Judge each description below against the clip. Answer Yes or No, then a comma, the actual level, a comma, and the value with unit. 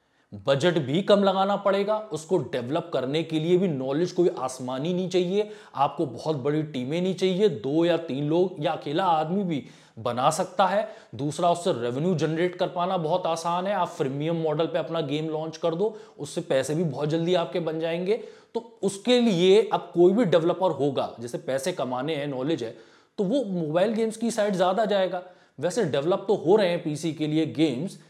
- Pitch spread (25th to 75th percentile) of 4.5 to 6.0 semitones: No, average, 3.5 semitones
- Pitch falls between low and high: Yes, medium, 175 Hz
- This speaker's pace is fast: Yes, fast, 195 wpm